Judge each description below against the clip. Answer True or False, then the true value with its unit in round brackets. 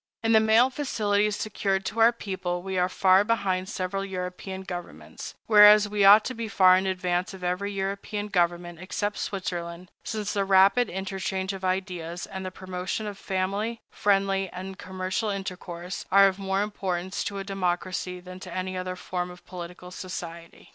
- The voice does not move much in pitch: True (1.8 semitones)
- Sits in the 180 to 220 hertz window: True (190 Hz)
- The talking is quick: False (170 wpm)